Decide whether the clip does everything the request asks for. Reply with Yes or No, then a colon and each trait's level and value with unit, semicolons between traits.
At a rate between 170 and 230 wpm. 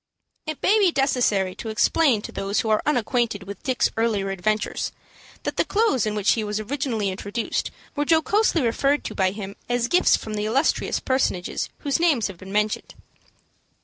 Yes: average, 180 wpm